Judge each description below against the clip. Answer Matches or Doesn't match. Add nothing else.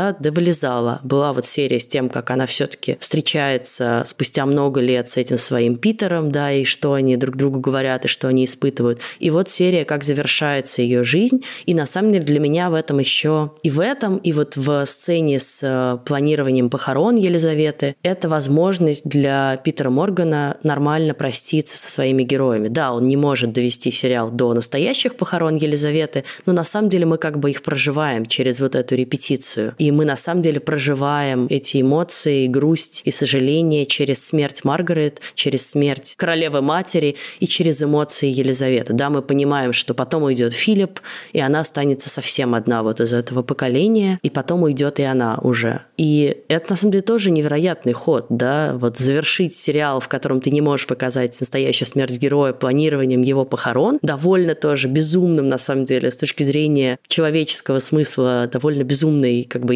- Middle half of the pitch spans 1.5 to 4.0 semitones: Matches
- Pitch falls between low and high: Matches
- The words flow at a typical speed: Doesn't match